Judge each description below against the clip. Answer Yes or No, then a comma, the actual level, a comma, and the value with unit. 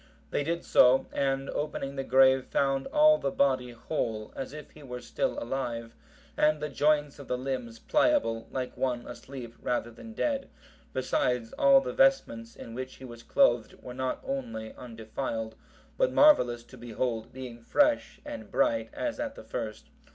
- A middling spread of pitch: Yes, average, 4.3 semitones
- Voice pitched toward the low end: Yes, low, 130 Hz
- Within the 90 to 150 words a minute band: No, average, 165 wpm